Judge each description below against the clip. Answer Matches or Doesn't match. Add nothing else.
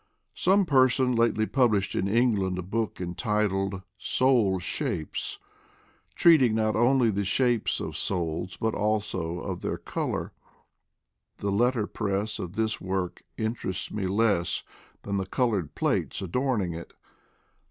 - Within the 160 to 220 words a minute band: Doesn't match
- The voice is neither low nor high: Doesn't match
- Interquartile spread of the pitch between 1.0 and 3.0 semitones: Doesn't match